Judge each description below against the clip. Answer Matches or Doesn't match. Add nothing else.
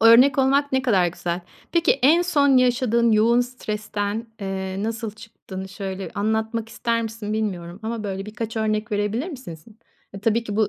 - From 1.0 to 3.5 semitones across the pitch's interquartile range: Matches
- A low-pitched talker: Doesn't match